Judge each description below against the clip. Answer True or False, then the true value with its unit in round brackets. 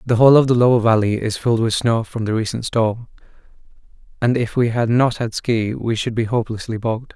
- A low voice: True (115 Hz)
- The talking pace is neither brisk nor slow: False (220 wpm)